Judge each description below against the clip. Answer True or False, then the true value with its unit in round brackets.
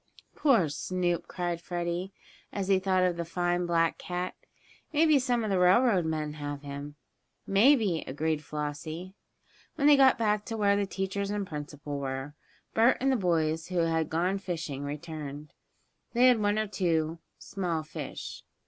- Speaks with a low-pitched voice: False (175 Hz)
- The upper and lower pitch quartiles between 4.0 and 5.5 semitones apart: True (4.4 semitones)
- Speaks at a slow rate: False (165 wpm)